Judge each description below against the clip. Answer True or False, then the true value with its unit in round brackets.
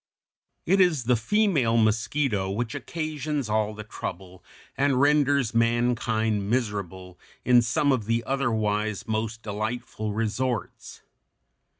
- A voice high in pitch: False (115 Hz)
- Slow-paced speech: True (115 wpm)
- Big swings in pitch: False (3.9 semitones)